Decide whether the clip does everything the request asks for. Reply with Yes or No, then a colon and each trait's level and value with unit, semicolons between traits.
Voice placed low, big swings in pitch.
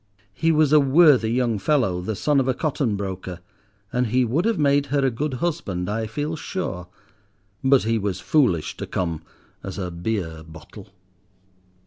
Yes: low, 120 Hz; wide, 7.4 semitones